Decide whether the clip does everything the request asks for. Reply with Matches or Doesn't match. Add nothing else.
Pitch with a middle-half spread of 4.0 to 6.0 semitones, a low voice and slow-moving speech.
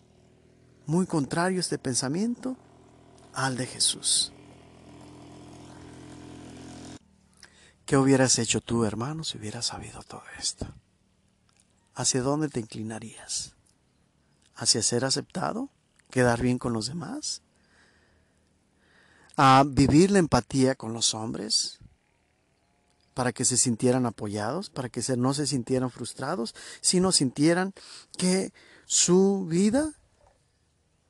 Matches